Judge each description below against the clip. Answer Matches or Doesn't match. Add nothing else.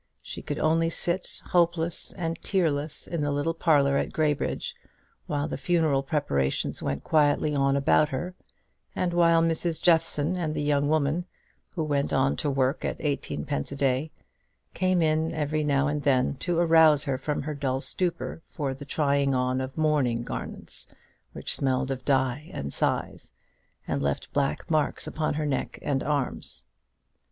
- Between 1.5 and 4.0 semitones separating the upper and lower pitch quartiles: Matches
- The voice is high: Doesn't match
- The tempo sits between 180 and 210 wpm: Doesn't match